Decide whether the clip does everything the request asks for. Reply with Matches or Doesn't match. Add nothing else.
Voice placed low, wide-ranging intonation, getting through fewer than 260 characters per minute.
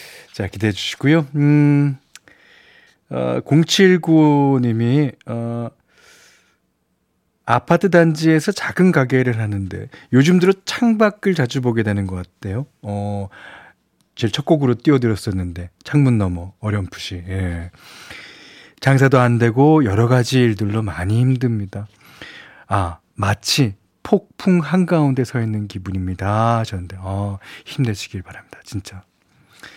Matches